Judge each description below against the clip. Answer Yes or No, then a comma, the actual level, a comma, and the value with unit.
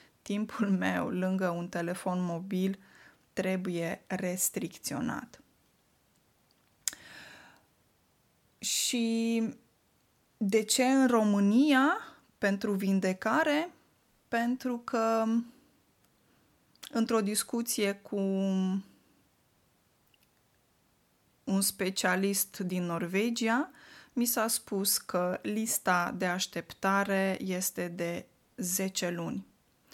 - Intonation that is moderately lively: Yes, average, 3.5 semitones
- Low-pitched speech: No, high, 200 Hz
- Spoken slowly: Yes, slow, 70 wpm